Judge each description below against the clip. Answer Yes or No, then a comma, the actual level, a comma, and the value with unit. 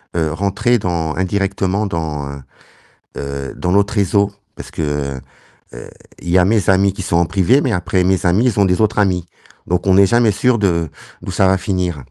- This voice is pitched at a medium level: No, very low, 95 Hz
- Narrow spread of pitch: No, average, 3.1 semitones